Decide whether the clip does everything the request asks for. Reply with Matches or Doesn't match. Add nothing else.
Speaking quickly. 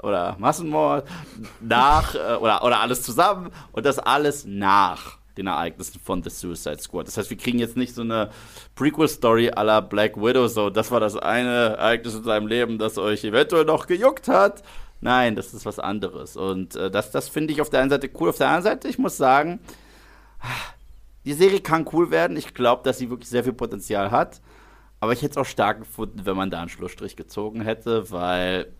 Matches